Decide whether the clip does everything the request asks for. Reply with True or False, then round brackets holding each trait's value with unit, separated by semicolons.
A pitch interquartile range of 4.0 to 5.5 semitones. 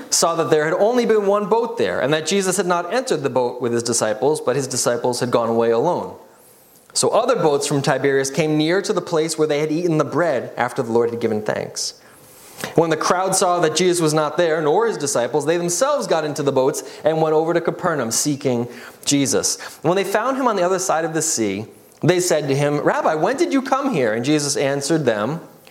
True (4.5 semitones)